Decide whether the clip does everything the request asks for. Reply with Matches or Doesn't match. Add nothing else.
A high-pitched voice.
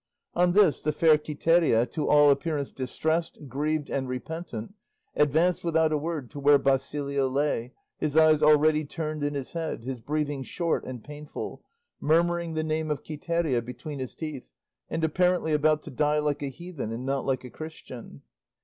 Doesn't match